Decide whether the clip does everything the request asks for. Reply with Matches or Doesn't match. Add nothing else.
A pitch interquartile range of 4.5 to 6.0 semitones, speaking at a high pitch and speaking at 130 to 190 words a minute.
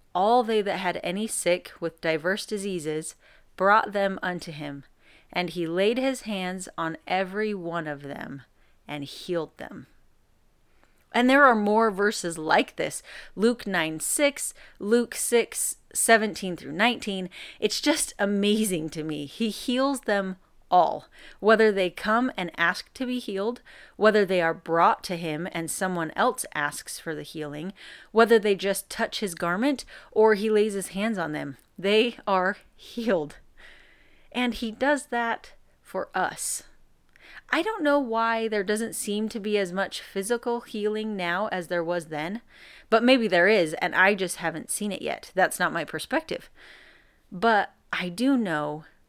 Matches